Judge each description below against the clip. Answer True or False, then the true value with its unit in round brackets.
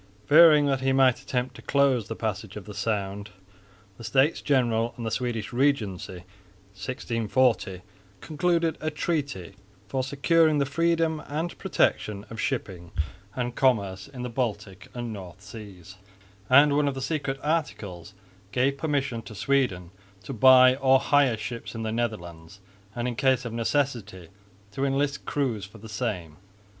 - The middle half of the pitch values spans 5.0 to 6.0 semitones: True (5.3 semitones)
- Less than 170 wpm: True (155 wpm)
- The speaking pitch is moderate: False (120 Hz)